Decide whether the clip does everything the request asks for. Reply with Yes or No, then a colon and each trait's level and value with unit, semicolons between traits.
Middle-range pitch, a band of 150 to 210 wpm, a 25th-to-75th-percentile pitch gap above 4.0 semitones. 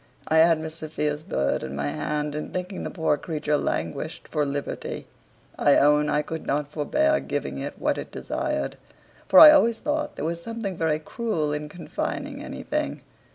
No: medium, 155 Hz; average, 175 wpm; average, 3.4 semitones